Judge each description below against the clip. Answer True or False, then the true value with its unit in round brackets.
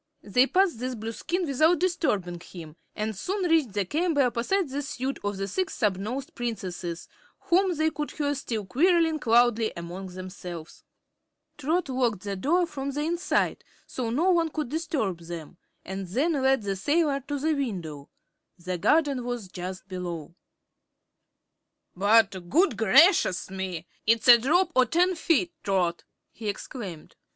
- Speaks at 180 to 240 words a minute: False (150 wpm)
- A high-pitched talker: True (245 Hz)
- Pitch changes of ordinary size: False (8.6 semitones)